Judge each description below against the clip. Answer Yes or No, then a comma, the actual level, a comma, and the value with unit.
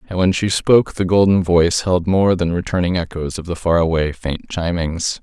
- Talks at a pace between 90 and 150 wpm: No, fast, 205 wpm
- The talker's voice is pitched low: Yes, very low, 90 Hz